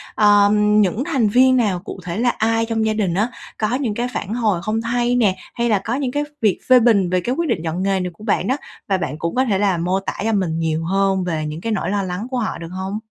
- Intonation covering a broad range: No, average, 4.0 semitones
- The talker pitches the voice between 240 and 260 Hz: No, high, 210 Hz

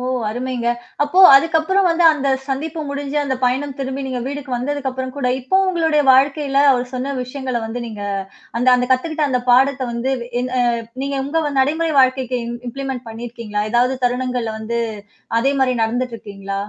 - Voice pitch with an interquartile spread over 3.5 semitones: No, narrow, 2.5 semitones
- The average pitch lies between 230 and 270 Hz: Yes, very high, 260 Hz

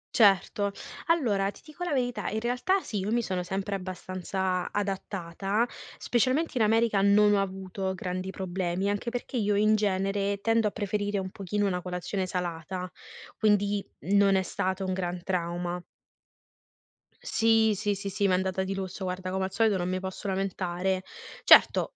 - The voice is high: Yes, high, 195 Hz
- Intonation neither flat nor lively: No, narrow, 2.0 semitones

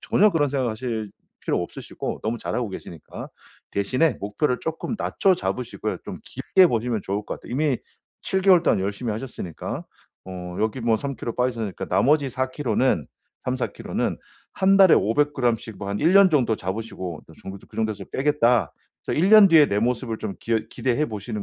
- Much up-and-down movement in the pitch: Yes, wide, 5.7 semitones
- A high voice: No, low, 120 Hz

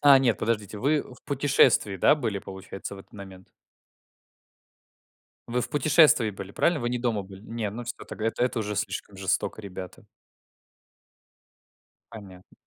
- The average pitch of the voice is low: Yes, low, 110 Hz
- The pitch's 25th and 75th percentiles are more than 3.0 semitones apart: Yes, average, 4.2 semitones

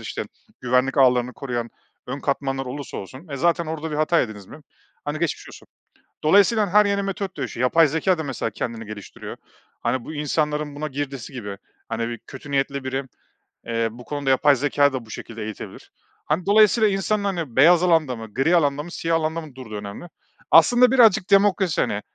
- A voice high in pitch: No, medium, 145 Hz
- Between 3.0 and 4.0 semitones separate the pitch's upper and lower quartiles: No, average, 5.2 semitones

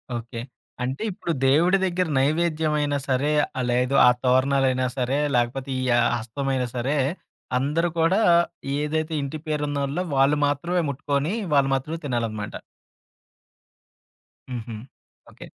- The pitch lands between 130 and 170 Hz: Yes, medium, 140 Hz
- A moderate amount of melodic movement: Yes, average, 3.2 semitones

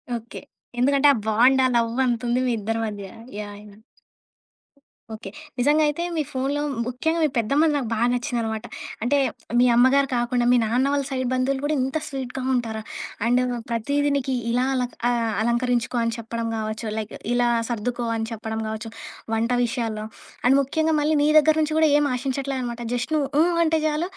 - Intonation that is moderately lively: Yes, average, 3.3 semitones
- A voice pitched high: Yes, high, 245 Hz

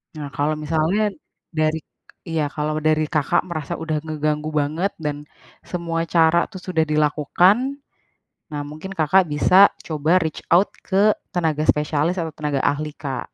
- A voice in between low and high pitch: Yes, medium, 155 Hz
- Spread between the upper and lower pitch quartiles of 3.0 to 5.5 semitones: No, narrow, 2.4 semitones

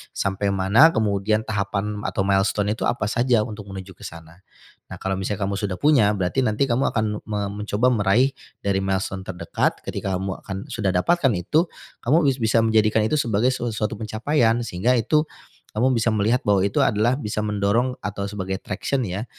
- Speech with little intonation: No, average, 3.3 semitones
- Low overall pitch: Yes, low, 105 Hz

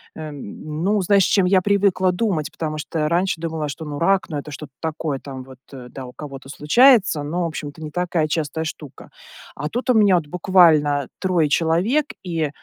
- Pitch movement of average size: Yes, average, 3.8 semitones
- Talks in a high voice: No, medium, 160 Hz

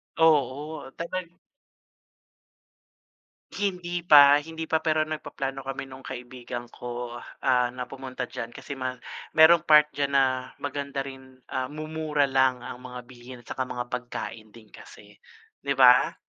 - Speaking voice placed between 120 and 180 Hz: Yes, low, 135 Hz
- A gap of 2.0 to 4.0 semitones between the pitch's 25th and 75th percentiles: Yes, average, 3.4 semitones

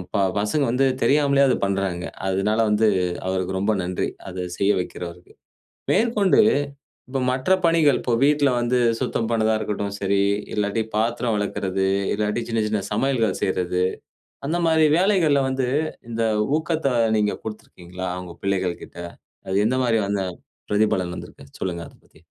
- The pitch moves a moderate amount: No, wide, 5.9 semitones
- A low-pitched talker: Yes, low, 110 Hz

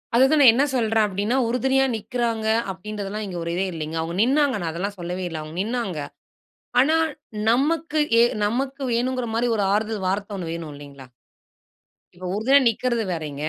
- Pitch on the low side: No, high, 215 Hz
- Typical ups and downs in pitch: No, wide, 6.0 semitones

